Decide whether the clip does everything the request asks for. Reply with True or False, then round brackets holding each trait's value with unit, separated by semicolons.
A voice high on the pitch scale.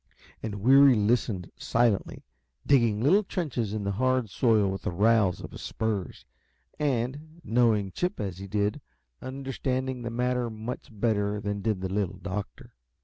False (110 Hz)